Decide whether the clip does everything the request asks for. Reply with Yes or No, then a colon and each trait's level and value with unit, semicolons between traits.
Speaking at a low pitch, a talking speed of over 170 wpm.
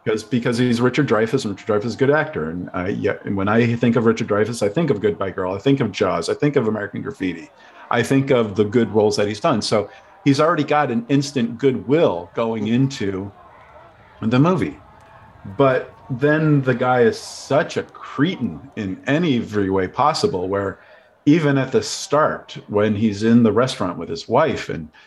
Yes: low, 120 Hz; average, 195 wpm